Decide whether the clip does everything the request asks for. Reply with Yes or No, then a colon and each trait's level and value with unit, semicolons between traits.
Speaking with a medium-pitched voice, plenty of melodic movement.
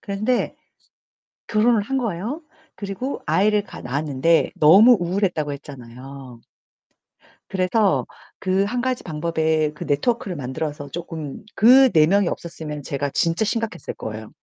Yes: medium, 170 Hz; wide, 6.3 semitones